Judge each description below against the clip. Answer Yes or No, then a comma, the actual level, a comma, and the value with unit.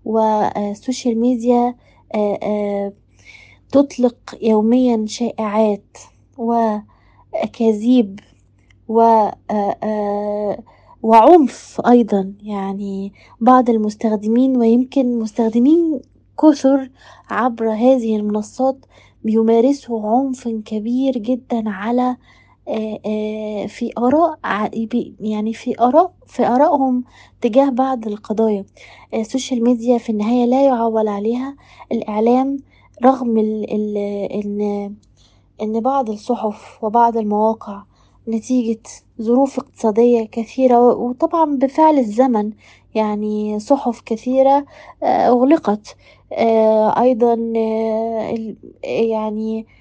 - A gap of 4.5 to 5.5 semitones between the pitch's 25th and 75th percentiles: No, average, 2.9 semitones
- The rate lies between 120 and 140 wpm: No, average, 75 wpm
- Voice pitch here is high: Yes, high, 230 Hz